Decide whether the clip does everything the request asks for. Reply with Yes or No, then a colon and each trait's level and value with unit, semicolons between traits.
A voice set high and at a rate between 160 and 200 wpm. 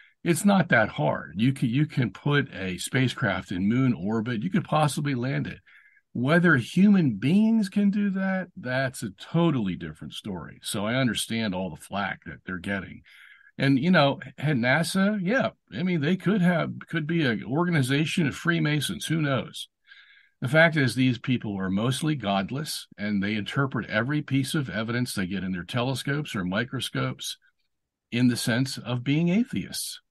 No: low, 135 Hz; average, 170 wpm